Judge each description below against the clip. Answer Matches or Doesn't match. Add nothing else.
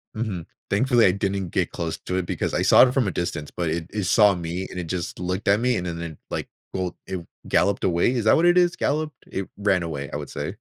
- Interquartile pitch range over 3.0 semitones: Matches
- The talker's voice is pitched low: Matches